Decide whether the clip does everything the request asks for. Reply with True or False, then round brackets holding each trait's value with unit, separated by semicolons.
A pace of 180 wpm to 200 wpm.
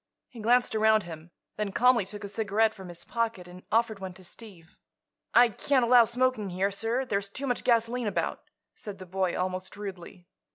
True (190 wpm)